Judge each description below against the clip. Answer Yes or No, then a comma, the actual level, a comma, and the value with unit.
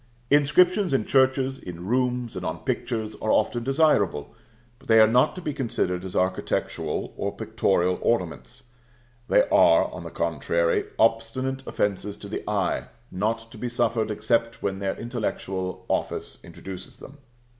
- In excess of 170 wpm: No, average, 150 wpm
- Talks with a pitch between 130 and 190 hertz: No, low, 115 Hz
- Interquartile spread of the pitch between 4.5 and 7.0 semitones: Yes, wide, 5.5 semitones